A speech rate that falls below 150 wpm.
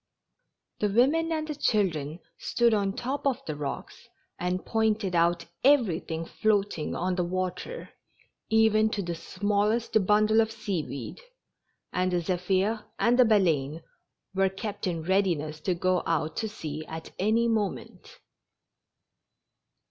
Yes: average, 140 wpm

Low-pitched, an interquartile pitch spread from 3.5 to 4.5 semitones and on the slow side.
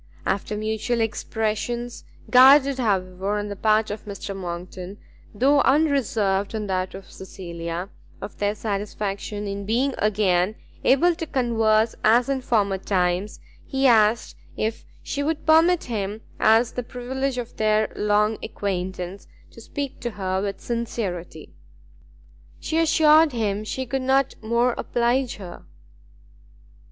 No: high, 215 Hz; average, 4.0 semitones; slow, 130 wpm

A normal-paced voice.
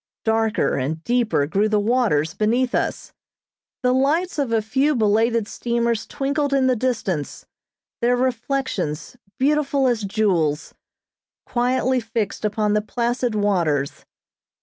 No: slow, 125 wpm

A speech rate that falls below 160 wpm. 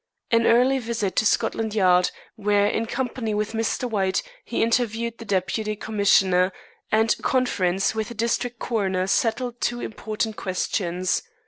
Yes: average, 145 wpm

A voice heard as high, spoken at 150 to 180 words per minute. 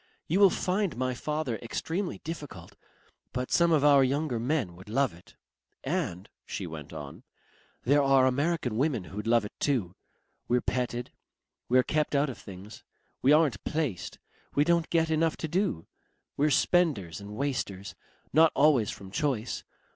No: low, 135 Hz; average, 155 wpm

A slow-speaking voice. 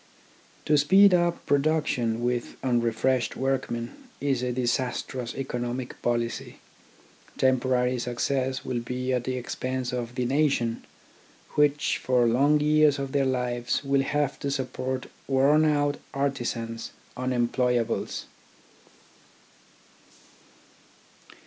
Yes: slow, 105 wpm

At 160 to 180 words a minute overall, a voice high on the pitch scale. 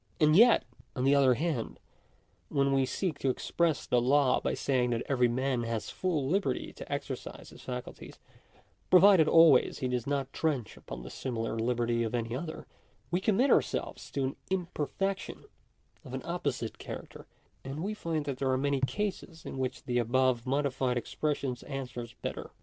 No: average, 170 wpm; low, 135 Hz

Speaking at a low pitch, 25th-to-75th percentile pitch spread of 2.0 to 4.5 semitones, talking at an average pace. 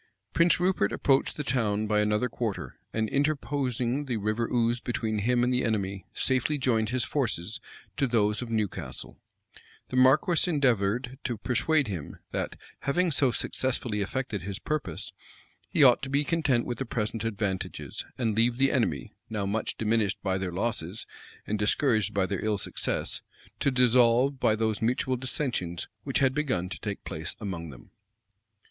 Yes: low, 115 Hz; average, 4.0 semitones; average, 165 wpm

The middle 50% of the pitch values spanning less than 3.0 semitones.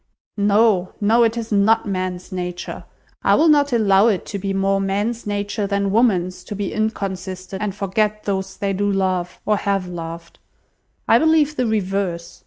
Yes: narrow, 2.5 semitones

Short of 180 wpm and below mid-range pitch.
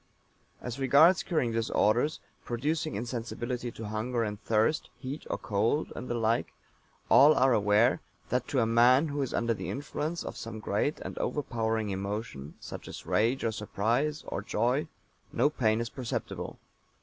Yes: average, 160 wpm; low, 120 Hz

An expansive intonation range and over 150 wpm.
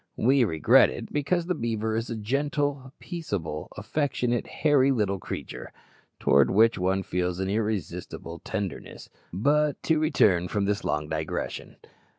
No: wide, 7.1 semitones; average, 140 wpm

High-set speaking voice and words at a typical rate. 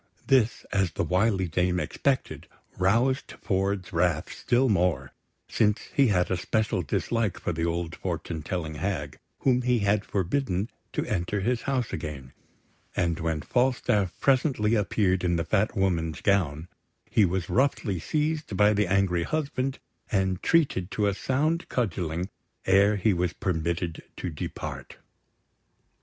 No: very low, 95 Hz; average, 145 wpm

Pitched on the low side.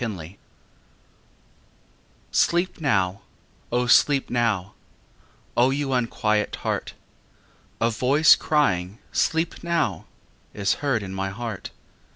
Yes: low, 120 Hz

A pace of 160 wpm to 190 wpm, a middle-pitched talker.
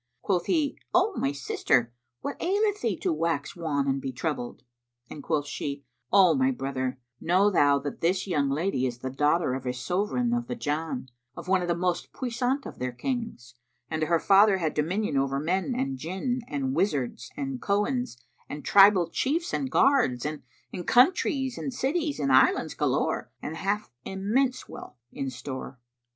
Yes: average, 170 wpm; medium, 170 Hz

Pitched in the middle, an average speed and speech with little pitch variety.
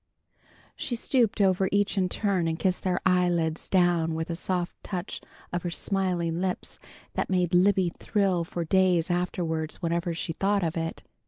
Yes: medium, 180 Hz; average, 165 wpm; narrow, 2.2 semitones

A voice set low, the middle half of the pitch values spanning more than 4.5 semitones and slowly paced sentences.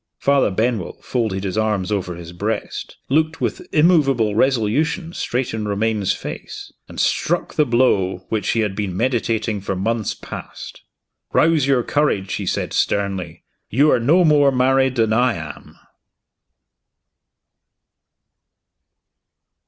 Yes: low, 115 Hz; average, 5.2 semitones; slow, 130 wpm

